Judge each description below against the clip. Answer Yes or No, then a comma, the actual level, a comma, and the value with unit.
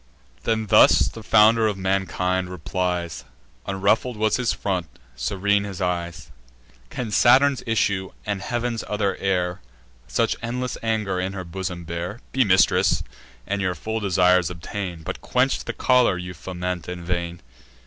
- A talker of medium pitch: No, very low, 95 Hz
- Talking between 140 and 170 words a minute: Yes, average, 145 wpm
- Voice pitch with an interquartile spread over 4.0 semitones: No, average, 3.4 semitones